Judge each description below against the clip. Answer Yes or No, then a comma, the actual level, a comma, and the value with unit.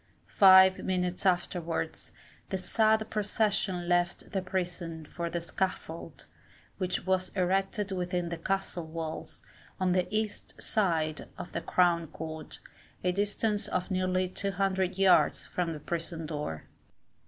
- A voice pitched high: No, medium, 180 Hz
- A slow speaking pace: Yes, slow, 130 wpm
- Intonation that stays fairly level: Yes, narrow, 2.2 semitones